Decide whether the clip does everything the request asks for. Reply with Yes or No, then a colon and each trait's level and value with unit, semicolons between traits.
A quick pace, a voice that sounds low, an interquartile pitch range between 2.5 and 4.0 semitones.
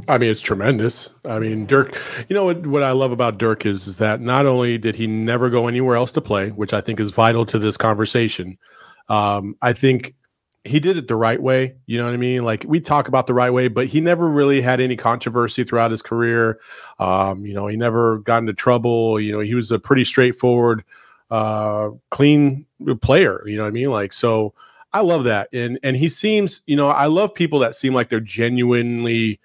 Yes: fast, 220 wpm; low, 120 Hz; average, 3.0 semitones